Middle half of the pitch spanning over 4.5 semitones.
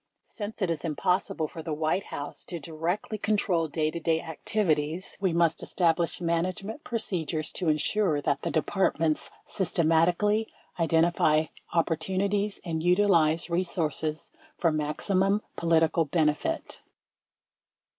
No: average, 3.2 semitones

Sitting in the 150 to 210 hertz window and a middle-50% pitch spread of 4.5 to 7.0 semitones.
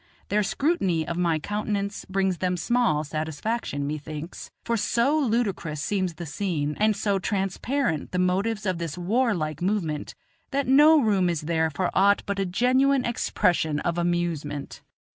Yes: medium, 185 Hz; average, 5.2 semitones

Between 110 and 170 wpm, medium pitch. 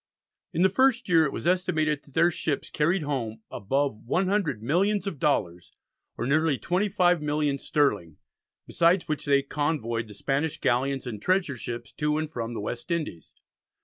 Yes: average, 165 wpm; medium, 150 Hz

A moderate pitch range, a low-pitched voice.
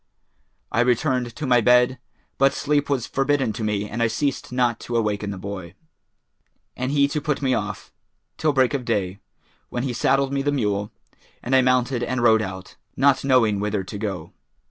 Yes: average, 4.4 semitones; low, 125 Hz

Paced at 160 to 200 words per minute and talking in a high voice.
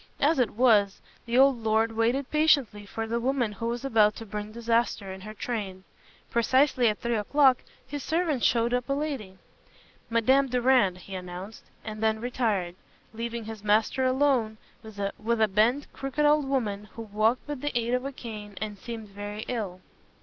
Yes: average, 175 wpm; high, 230 Hz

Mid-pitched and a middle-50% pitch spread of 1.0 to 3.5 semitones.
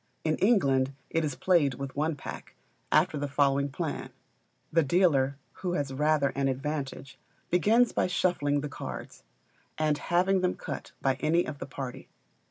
No: medium, 145 Hz; average, 4.0 semitones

